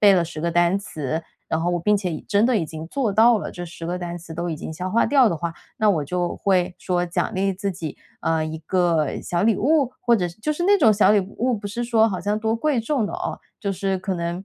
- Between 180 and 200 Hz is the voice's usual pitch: Yes, high, 190 Hz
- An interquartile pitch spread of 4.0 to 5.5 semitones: Yes, average, 4.4 semitones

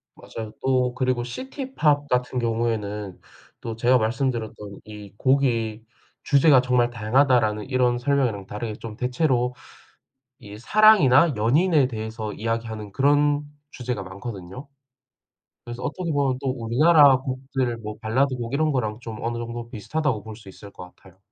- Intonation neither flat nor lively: Yes, average, 3.6 semitones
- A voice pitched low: Yes, low, 120 Hz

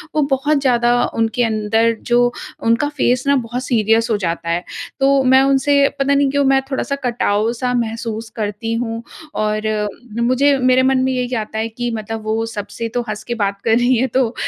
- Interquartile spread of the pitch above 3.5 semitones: No, average, 2.7 semitones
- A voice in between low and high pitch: No, high, 240 Hz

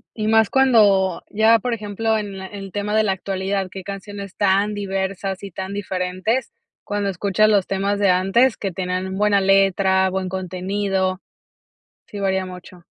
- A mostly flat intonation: Yes, narrow, 1.5 semitones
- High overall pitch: Yes, high, 195 Hz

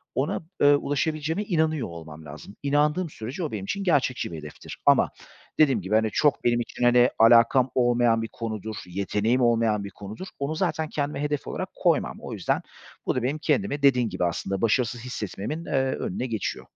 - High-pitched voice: No, low, 120 Hz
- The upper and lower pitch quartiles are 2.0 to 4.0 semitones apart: No, average, 5.3 semitones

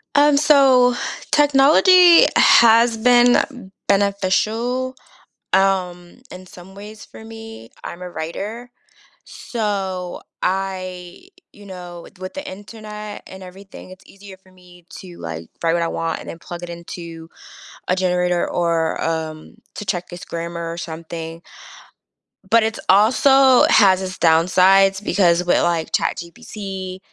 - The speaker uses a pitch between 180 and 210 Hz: Yes, high, 190 Hz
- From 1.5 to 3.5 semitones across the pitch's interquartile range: No, average, 4.2 semitones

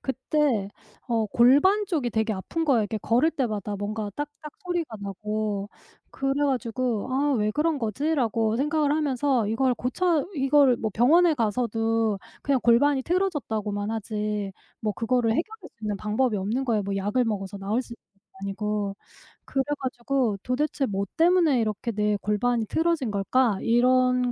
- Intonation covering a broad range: No, average, 4.8 semitones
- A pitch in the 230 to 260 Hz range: Yes, high, 240 Hz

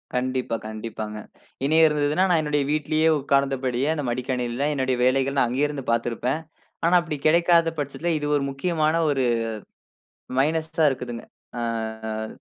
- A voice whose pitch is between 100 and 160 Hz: Yes, medium, 140 Hz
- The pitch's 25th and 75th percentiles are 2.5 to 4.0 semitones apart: Yes, average, 3.6 semitones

